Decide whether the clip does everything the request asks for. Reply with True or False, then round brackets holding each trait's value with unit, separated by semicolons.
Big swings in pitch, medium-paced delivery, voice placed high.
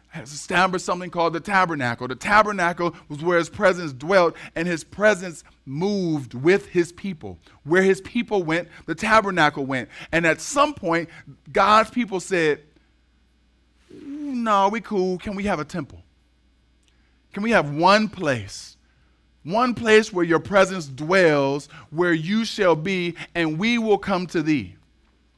False (5.8 semitones; 150 wpm; 170 Hz)